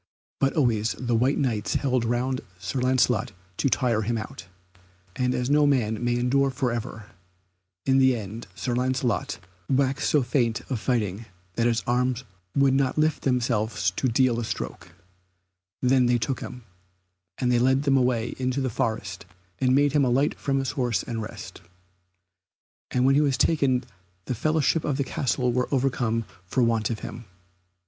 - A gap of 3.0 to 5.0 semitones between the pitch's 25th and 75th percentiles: No, narrow, 2.4 semitones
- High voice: No, low, 125 Hz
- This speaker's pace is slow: No, average, 170 wpm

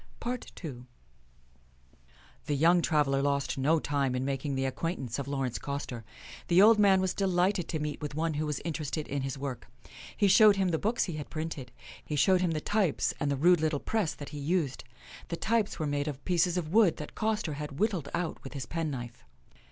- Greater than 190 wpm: Yes, average, 200 wpm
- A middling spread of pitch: Yes, average, 4.3 semitones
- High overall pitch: No, medium, 155 Hz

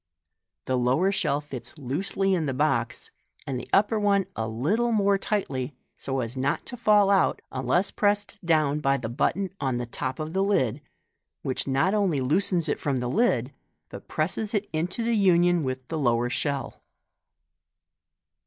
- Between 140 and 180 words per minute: Yes, average, 165 wpm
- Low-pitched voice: No, medium, 155 Hz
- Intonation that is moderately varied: No, wide, 7.3 semitones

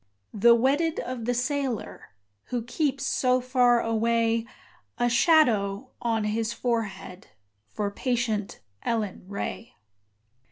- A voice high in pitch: Yes, high, 235 Hz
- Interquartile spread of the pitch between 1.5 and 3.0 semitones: Yes, narrow, 2.4 semitones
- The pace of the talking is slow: Yes, slow, 110 wpm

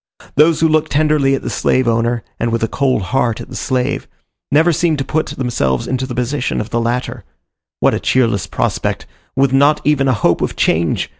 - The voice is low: Yes, low, 130 Hz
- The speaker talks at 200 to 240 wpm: Yes, fast, 205 wpm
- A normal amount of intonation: Yes, average, 3.9 semitones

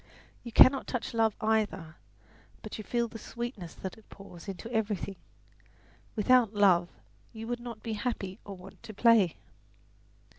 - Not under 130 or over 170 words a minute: Yes, average, 150 wpm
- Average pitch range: Yes, average, 3.1 semitones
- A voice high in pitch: Yes, high, 215 Hz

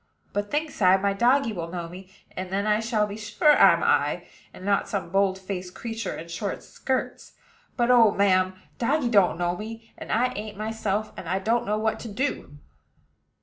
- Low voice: No, high, 205 Hz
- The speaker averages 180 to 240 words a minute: Yes, average, 190 wpm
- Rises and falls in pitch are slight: No, average, 3.2 semitones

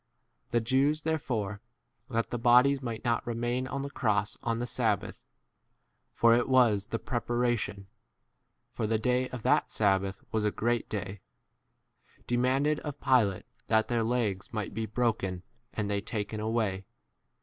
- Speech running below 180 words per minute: Yes, average, 160 wpm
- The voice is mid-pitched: No, low, 115 Hz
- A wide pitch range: No, average, 2.9 semitones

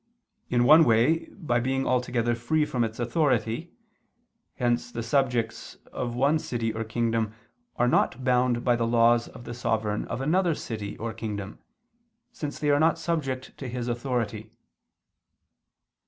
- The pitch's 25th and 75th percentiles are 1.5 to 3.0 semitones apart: Yes, narrow, 2.6 semitones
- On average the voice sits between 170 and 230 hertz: No, low, 120 Hz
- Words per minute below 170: Yes, average, 150 wpm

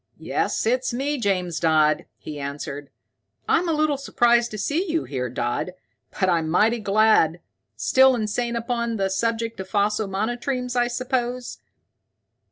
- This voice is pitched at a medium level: No, high, 225 Hz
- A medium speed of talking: Yes, average, 145 wpm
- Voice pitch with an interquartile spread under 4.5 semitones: No, wide, 5.4 semitones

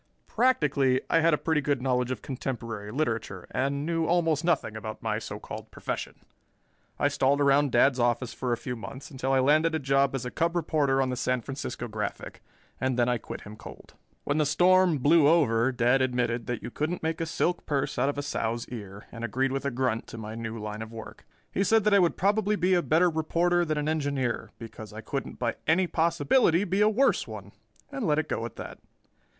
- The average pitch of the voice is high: No, low, 135 Hz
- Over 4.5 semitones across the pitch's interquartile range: Yes, average, 5.2 semitones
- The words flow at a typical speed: No, fast, 220 wpm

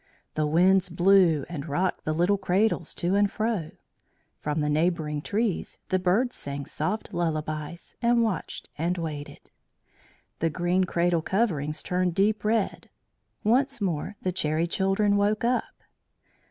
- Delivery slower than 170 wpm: Yes, average, 140 wpm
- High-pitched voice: No, medium, 180 Hz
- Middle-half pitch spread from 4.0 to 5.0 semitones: Yes, average, 4.4 semitones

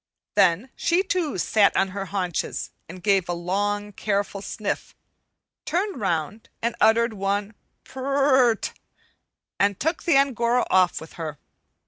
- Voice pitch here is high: Yes, high, 205 Hz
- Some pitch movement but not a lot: Yes, average, 4.9 semitones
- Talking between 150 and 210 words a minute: No, average, 140 wpm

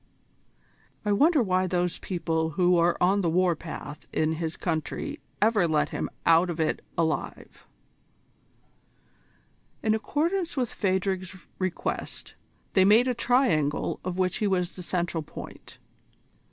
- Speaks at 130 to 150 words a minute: Yes, slow, 135 wpm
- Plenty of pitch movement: No, average, 3.5 semitones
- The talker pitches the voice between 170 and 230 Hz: Yes, medium, 185 Hz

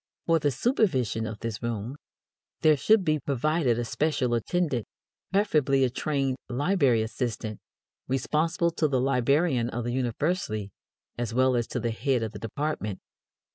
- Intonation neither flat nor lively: Yes, average, 4.8 semitones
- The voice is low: Yes, low, 130 Hz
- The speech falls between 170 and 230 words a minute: No, average, 150 wpm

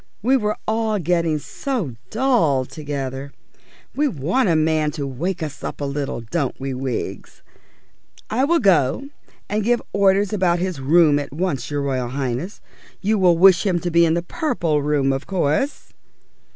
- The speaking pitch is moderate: Yes, medium, 170 Hz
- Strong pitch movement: Yes, wide, 6.1 semitones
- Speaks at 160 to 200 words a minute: Yes, average, 165 wpm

